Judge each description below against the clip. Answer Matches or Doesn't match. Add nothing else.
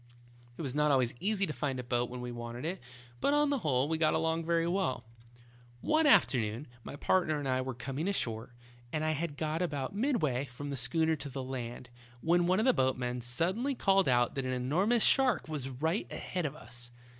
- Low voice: Doesn't match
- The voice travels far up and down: Matches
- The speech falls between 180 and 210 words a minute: Matches